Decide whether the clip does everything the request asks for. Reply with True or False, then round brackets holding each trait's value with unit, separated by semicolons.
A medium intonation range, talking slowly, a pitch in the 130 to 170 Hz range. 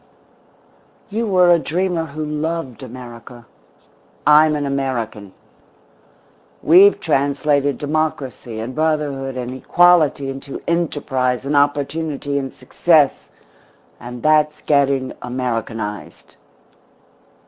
True (3.4 semitones; 95 wpm; 140 Hz)